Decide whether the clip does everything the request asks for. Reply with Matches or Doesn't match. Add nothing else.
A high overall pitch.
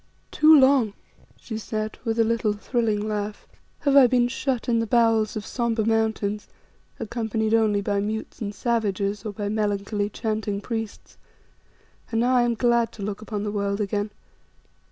Matches